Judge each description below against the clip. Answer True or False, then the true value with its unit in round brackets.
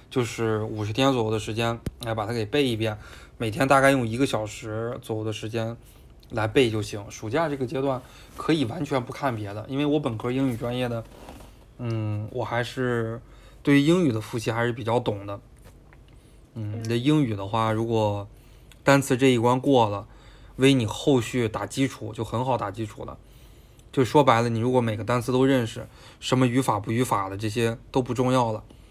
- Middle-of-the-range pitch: False (115 Hz)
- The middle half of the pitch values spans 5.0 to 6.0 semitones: False (3.0 semitones)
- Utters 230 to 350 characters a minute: True (280 characters per minute)